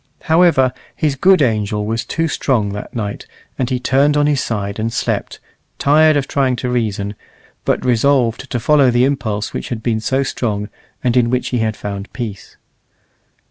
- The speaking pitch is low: Yes, low, 125 Hz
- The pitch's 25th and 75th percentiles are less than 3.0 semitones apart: No, average, 4.2 semitones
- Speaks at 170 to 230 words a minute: Yes, average, 180 wpm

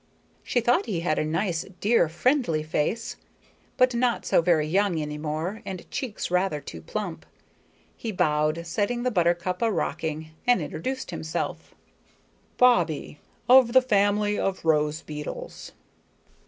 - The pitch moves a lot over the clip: Yes, wide, 6.8 semitones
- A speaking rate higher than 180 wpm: No, average, 140 wpm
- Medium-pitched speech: Yes, medium, 180 Hz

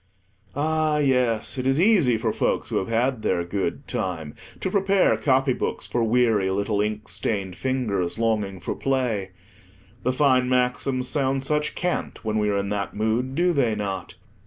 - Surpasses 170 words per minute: No, average, 160 wpm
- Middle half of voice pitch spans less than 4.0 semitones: No, average, 4.5 semitones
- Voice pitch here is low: Yes, low, 125 Hz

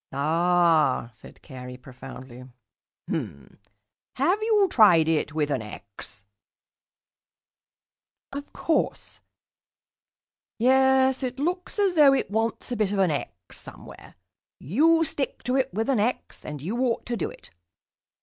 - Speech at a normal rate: No, slow, 130 wpm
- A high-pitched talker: Yes, high, 215 Hz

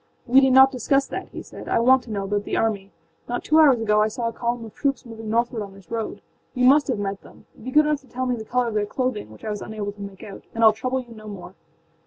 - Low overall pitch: No, high, 230 Hz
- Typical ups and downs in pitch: Yes, average, 3.5 semitones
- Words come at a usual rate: No, fast, 290 wpm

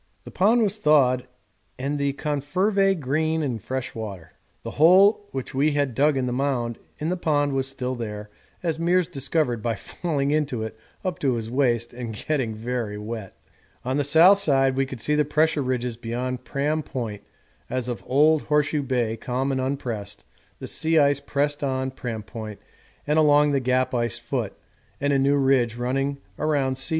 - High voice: No, low, 135 Hz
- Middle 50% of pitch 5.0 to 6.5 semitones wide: No, average, 3.5 semitones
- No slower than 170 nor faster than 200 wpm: Yes, average, 180 wpm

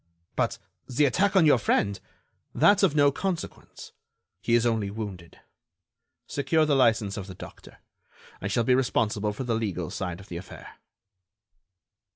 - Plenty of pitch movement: Yes, wide, 6.0 semitones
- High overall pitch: No, low, 115 Hz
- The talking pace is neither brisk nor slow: Yes, average, 155 wpm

